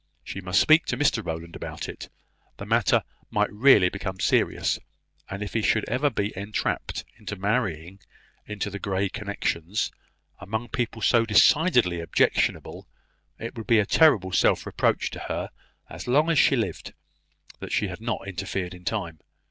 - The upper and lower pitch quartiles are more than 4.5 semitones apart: No, average, 3.7 semitones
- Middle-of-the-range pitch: No, low, 105 Hz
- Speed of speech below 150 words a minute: No, average, 165 wpm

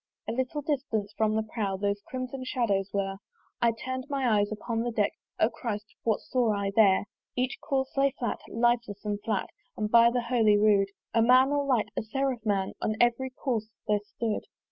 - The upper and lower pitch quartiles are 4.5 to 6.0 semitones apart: No, average, 3.5 semitones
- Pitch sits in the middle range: No, high, 230 Hz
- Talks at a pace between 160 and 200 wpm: Yes, average, 190 wpm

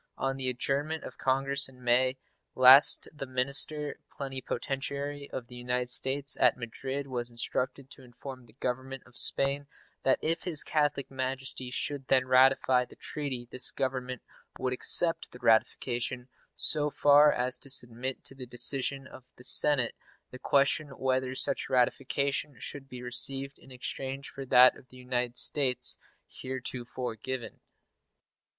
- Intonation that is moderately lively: No, narrow, 1.6 semitones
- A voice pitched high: No, low, 130 Hz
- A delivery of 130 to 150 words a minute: Yes, average, 145 wpm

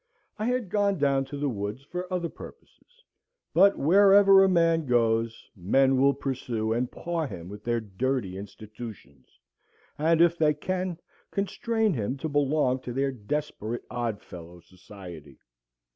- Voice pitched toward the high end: No, low, 135 Hz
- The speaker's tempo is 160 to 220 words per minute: No, average, 145 wpm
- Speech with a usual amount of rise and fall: No, wide, 7.7 semitones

